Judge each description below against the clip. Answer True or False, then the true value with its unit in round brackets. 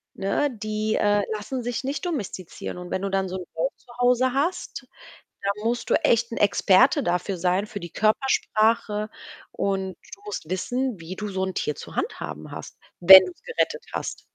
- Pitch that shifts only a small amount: False (4.4 semitones)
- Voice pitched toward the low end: False (210 Hz)